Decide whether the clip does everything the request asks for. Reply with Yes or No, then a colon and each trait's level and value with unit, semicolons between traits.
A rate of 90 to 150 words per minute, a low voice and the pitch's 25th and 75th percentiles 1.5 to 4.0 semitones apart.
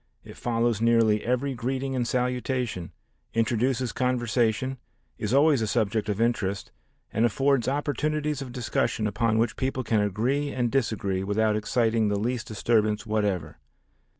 Yes: average, 140 wpm; low, 115 Hz; average, 3.1 semitones